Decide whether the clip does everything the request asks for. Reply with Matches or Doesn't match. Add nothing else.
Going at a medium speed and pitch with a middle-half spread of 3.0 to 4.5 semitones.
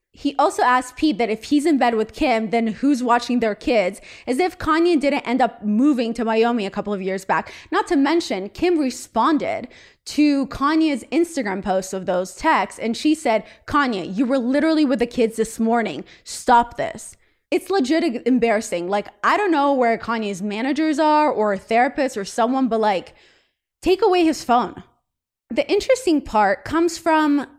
Doesn't match